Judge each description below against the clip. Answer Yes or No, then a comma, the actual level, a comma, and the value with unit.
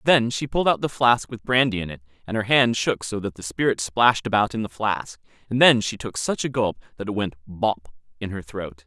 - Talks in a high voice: No, low, 110 Hz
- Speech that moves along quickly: Yes, fast, 250 wpm